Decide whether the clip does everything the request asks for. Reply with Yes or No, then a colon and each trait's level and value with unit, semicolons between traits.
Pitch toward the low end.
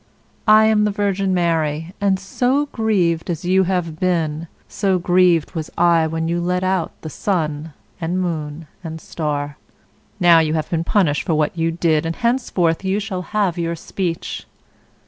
No: medium, 175 Hz